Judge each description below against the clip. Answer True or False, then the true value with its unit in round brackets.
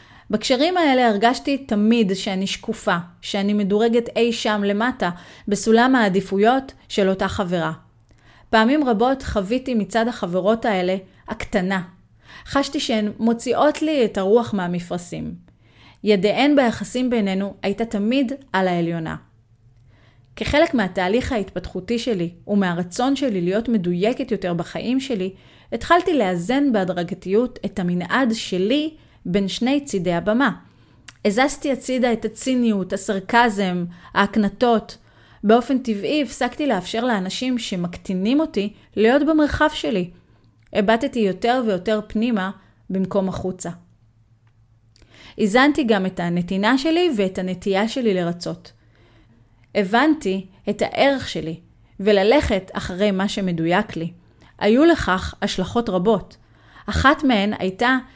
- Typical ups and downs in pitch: True (4.6 semitones)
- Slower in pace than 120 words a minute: True (110 wpm)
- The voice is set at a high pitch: True (210 Hz)